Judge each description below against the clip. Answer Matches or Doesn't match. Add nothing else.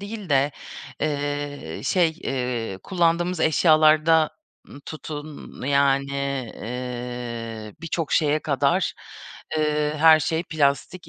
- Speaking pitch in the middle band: Matches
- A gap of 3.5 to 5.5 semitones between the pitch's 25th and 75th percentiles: Doesn't match